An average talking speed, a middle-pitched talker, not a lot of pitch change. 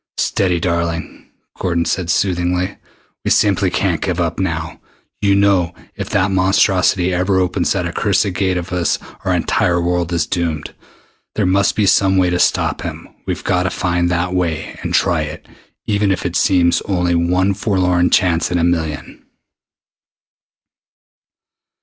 No: average, 155 wpm; very low, 90 Hz; narrow, 1.7 semitones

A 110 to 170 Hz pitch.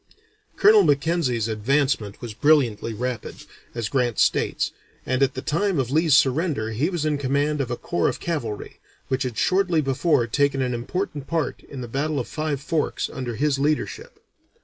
Yes: medium, 140 Hz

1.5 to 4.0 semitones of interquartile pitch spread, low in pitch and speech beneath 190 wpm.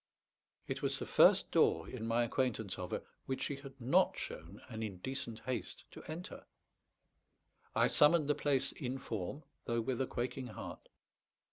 Yes: average, 3.5 semitones; low, 125 Hz; average, 160 wpm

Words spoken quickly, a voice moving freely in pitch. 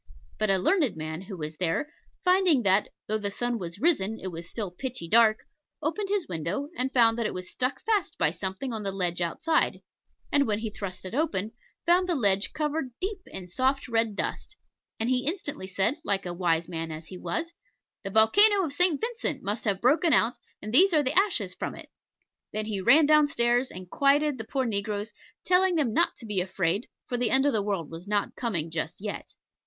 Yes: fast, 210 wpm; wide, 7.4 semitones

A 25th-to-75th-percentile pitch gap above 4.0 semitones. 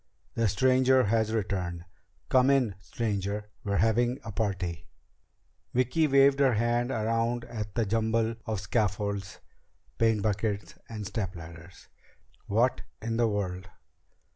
No: average, 3.1 semitones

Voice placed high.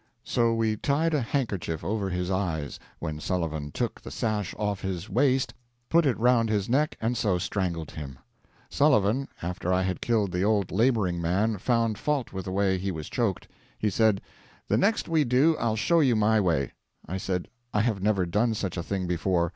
No: low, 105 Hz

